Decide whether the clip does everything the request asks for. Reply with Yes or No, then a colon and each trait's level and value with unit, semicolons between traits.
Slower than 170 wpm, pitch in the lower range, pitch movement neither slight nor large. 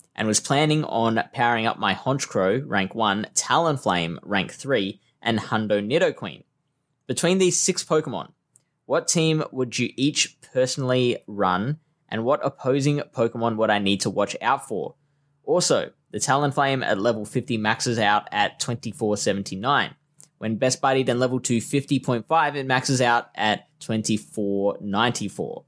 Yes: average, 140 wpm; low, 125 Hz; average, 4.7 semitones